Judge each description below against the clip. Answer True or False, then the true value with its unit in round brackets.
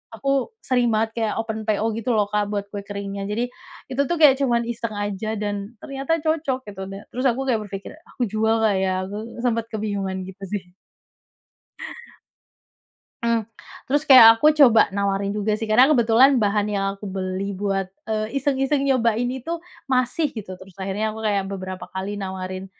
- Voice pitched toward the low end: False (215 Hz)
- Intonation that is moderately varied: True (3.8 semitones)